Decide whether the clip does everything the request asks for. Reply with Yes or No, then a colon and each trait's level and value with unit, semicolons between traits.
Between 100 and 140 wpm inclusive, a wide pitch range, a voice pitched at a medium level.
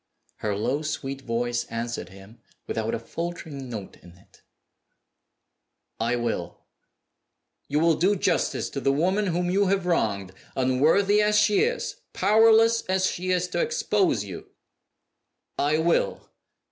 Yes: slow, 135 wpm; wide, 8.8 semitones; medium, 155 Hz